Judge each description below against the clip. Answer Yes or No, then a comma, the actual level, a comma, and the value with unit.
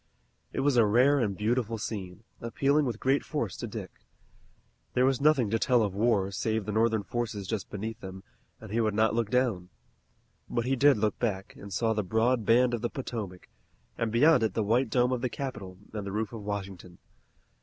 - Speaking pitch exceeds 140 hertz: No, low, 110 Hz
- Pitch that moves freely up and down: No, average, 3.4 semitones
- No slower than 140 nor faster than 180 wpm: No, fast, 205 wpm